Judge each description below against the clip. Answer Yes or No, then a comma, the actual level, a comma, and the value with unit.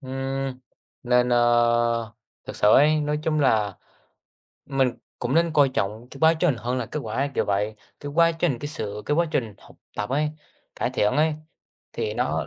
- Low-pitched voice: Yes, low, 130 Hz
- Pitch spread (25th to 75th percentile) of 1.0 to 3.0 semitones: No, average, 4.3 semitones